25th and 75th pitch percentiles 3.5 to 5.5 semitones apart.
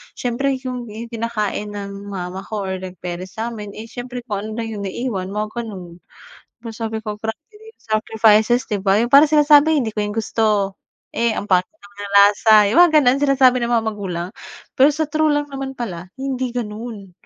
Yes: average, 3.9 semitones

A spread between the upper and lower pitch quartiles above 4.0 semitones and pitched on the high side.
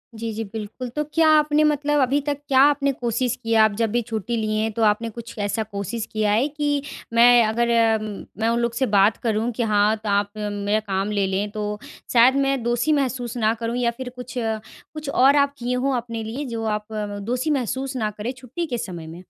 No: average, 3.2 semitones; high, 230 Hz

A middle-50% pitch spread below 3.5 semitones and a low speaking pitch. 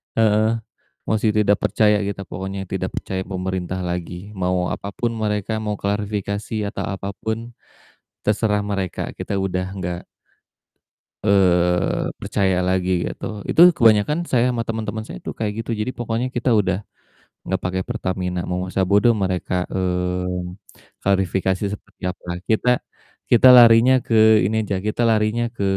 Yes: average, 2.9 semitones; low, 100 Hz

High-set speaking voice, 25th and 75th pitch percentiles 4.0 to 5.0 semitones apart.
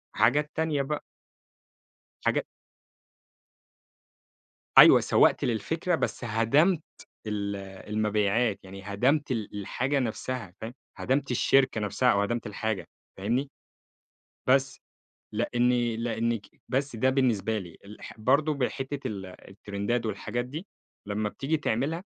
No: low, 120 Hz; average, 4.5 semitones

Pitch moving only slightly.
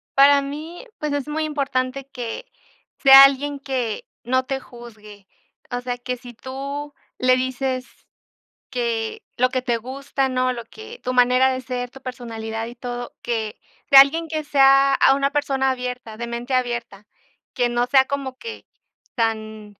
Yes: narrow, 2.2 semitones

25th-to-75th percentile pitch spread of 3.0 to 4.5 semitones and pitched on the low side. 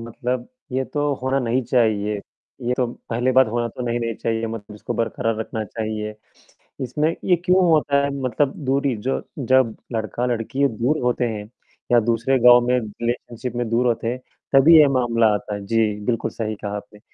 No: narrow, 2.6 semitones; low, 120 Hz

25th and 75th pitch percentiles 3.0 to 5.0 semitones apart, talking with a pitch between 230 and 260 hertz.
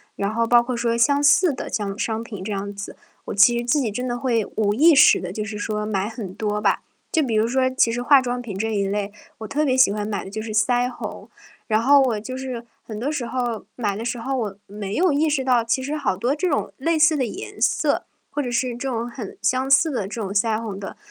Yes: average, 3.7 semitones; high, 235 Hz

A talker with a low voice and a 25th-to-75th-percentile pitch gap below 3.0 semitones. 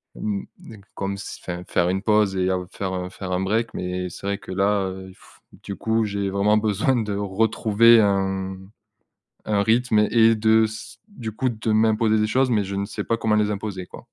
Yes: low, 105 Hz; narrow, 2.5 semitones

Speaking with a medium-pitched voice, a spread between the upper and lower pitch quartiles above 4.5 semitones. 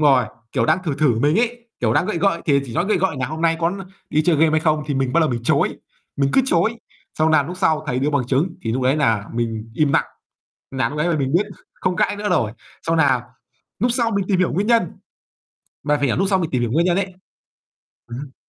Yes: medium, 155 Hz; average, 5.1 semitones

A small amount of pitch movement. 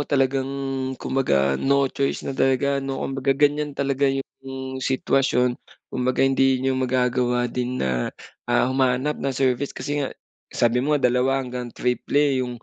Yes: narrow, 1.6 semitones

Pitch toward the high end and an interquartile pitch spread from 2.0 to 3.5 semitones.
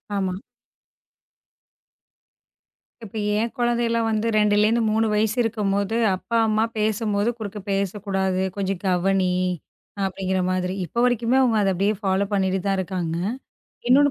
Yes: high, 205 Hz; average, 2.8 semitones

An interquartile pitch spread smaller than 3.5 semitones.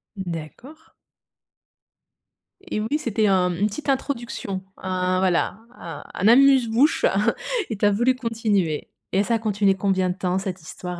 No: average, 4.2 semitones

